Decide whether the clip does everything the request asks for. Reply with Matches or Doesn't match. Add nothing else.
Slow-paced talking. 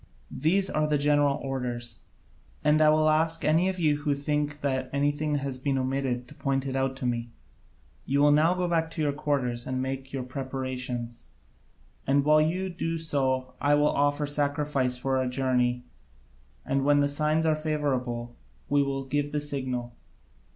Doesn't match